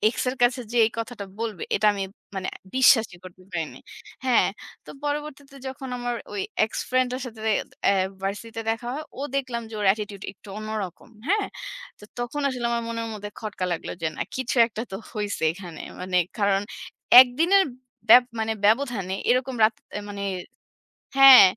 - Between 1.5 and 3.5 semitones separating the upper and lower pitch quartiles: No, average, 4.1 semitones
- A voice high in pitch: Yes, high, 230 Hz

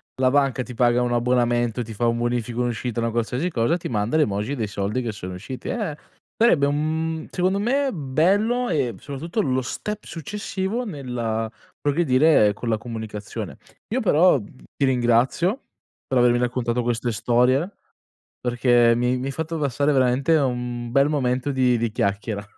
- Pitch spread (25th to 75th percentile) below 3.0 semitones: No, average, 4.1 semitones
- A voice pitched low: Yes, low, 125 Hz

